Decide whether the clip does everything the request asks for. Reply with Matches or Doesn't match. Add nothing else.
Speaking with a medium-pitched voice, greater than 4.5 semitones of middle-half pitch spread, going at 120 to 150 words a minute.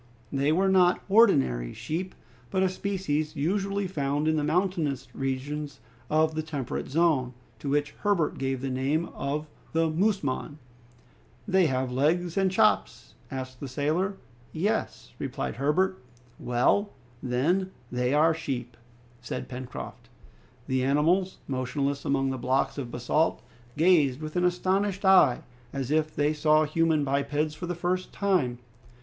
Matches